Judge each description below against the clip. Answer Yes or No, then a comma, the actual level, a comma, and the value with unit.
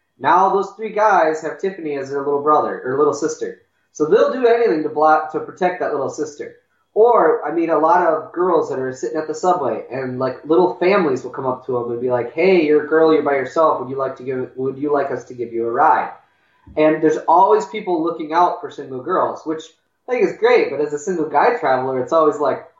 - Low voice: No, medium, 155 Hz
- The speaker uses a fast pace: Yes, fast, 245 wpm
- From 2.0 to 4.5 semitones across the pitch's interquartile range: No, wide, 5.4 semitones